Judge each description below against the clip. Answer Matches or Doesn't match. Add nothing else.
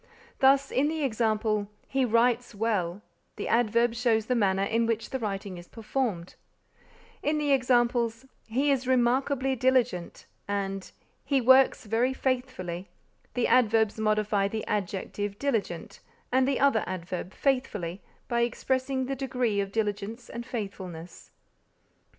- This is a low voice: Doesn't match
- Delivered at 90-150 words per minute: Matches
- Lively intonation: Doesn't match